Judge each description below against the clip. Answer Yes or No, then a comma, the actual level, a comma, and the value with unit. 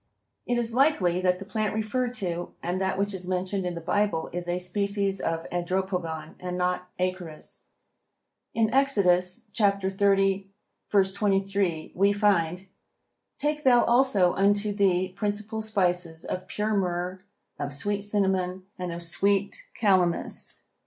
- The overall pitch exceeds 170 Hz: Yes, high, 190 Hz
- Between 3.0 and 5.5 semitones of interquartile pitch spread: No, narrow, 2.4 semitones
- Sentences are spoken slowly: Yes, slow, 130 wpm